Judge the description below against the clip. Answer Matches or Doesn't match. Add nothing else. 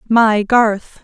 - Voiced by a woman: Matches